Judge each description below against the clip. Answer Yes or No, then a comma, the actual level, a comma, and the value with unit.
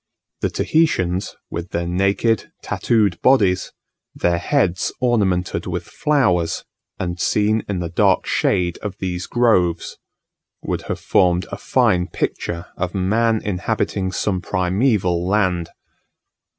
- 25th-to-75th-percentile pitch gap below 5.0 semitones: Yes, average, 3.4 semitones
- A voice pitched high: No, very low, 95 Hz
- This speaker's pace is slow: Yes, slow, 120 wpm